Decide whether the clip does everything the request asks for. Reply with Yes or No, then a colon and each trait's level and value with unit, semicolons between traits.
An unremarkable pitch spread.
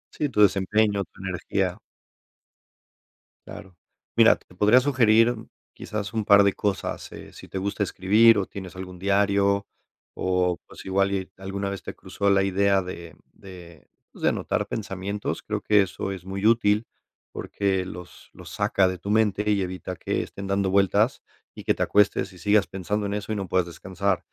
No: narrow, 1.7 semitones